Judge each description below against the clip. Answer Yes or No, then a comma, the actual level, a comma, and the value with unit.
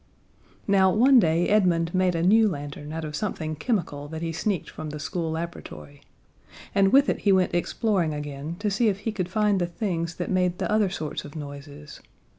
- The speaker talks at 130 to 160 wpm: No, average, 200 wpm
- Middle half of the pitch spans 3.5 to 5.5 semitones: Yes, average, 4.3 semitones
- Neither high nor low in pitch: Yes, medium, 175 Hz